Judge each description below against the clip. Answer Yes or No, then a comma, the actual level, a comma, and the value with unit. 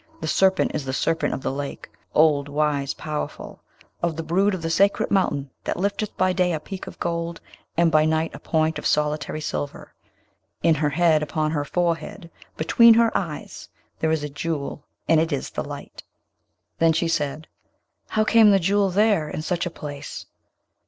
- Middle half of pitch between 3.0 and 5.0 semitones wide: Yes, average, 3.3 semitones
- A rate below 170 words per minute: No, average, 185 wpm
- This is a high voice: No, medium, 160 Hz